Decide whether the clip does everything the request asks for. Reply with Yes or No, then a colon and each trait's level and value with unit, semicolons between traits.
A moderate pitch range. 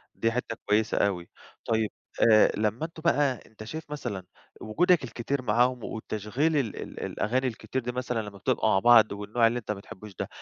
Yes: average, 3.3 semitones